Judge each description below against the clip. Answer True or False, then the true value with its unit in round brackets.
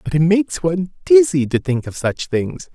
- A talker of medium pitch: True (165 Hz)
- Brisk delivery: True (220 wpm)